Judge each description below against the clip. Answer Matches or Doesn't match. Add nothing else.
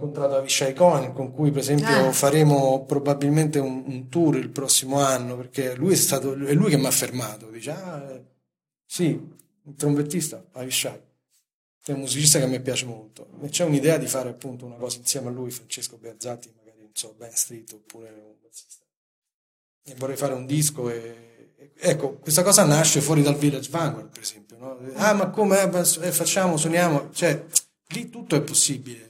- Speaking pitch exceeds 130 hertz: Matches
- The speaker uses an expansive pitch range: Doesn't match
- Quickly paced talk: Matches